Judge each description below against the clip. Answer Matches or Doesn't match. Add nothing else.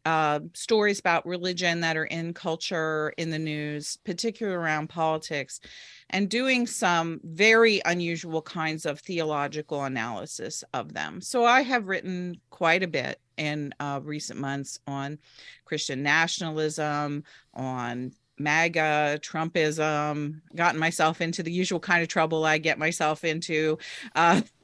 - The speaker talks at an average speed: Doesn't match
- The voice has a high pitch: Doesn't match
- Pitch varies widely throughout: Doesn't match